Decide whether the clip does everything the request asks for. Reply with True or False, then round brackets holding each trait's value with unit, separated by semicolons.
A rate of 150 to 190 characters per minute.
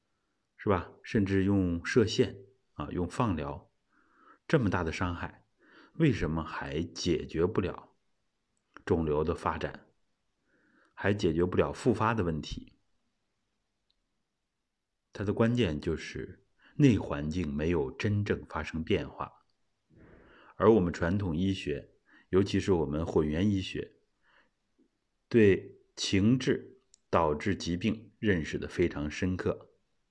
True (175 characters per minute)